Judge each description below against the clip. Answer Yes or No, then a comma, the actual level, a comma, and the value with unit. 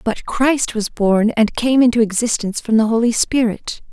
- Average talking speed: Yes, average, 185 wpm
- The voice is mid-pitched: No, high, 230 Hz